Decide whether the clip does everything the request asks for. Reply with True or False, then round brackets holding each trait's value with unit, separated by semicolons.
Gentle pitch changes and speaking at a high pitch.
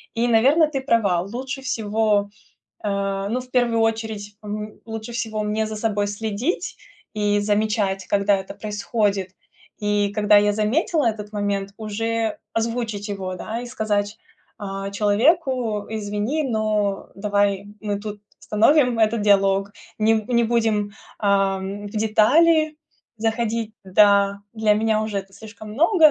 True (2.0 semitones; 215 Hz)